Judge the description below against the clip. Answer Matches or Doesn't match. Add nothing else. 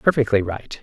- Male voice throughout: Matches